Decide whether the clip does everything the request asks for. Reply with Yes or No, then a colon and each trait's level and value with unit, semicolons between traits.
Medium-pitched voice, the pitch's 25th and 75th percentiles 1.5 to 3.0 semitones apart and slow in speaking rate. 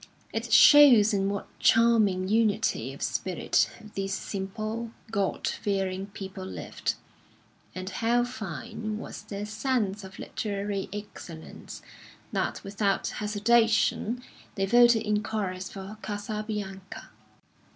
No: high, 210 Hz; narrow, 2.5 semitones; slow, 110 wpm